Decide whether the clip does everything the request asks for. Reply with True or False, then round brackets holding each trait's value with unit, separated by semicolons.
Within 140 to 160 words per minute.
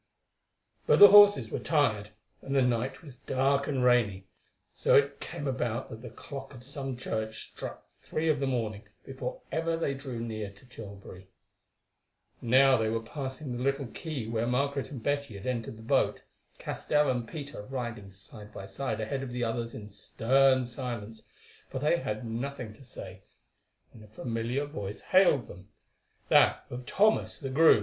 False (170 wpm)